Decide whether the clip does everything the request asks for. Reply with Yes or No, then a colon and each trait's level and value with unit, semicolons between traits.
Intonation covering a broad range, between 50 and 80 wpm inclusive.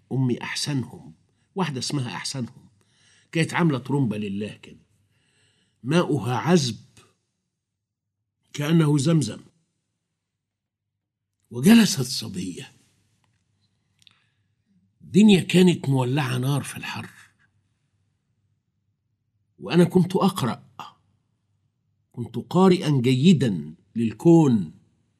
Yes: wide, 5.8 semitones; average, 70 wpm